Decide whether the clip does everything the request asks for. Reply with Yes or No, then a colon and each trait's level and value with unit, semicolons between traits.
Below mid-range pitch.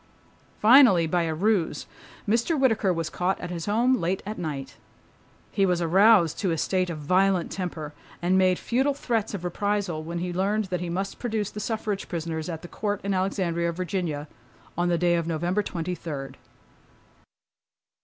No: medium, 180 Hz